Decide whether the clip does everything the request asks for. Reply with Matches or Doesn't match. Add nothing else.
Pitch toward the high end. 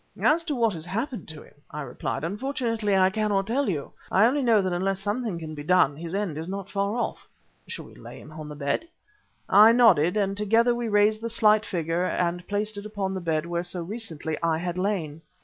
Matches